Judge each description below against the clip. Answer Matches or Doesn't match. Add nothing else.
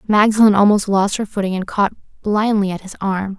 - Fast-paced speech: Doesn't match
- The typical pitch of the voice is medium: Doesn't match